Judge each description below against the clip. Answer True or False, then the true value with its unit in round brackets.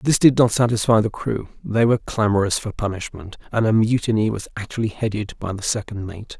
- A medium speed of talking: True (195 wpm)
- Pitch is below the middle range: True (110 Hz)